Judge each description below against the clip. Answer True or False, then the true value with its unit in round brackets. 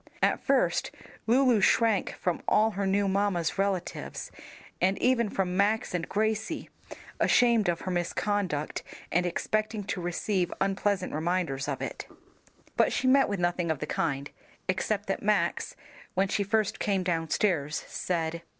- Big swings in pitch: False (3.3 semitones)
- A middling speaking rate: True (145 wpm)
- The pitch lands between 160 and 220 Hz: True (190 Hz)